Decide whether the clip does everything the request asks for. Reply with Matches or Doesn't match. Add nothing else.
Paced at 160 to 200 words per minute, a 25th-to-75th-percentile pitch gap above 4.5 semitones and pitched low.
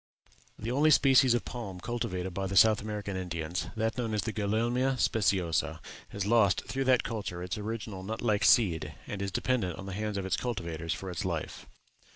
Doesn't match